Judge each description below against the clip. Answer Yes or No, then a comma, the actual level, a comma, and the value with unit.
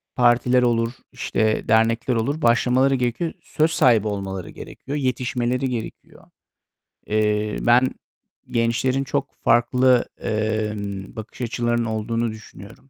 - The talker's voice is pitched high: No, low, 120 Hz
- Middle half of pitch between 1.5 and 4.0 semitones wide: Yes, narrow, 2.6 semitones